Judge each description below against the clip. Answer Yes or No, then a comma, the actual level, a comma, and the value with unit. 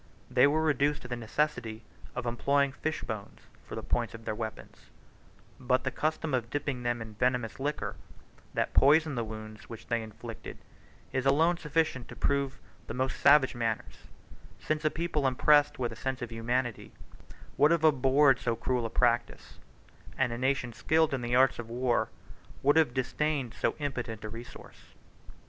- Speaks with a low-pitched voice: Yes, low, 130 Hz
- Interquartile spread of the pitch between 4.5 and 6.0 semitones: No, average, 3.7 semitones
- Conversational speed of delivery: Yes, average, 175 wpm